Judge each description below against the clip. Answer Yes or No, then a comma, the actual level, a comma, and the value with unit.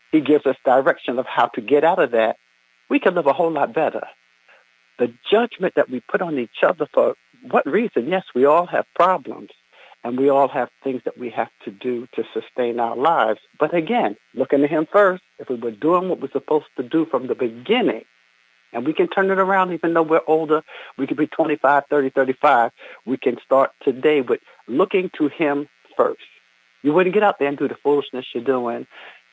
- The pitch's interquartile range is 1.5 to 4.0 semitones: No, wide, 5.5 semitones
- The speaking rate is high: Yes, fast, 210 wpm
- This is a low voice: No, medium, 145 Hz